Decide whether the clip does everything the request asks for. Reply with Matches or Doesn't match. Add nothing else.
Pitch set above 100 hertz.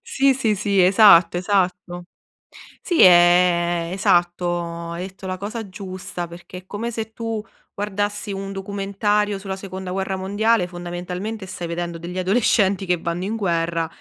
Matches